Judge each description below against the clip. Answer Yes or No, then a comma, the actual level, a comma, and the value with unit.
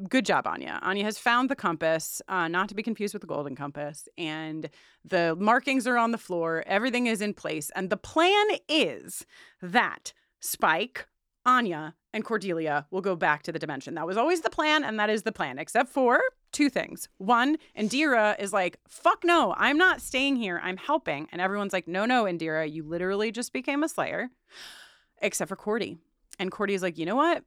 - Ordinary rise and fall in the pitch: No, wide, 6.9 semitones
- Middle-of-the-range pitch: No, high, 210 Hz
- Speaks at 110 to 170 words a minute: No, average, 200 wpm